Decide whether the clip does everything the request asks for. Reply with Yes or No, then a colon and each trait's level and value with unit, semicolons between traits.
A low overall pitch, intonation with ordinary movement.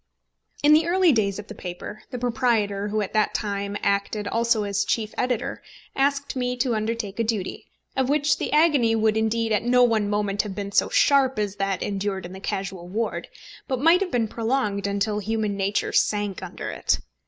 No: high, 215 Hz; average, 3.6 semitones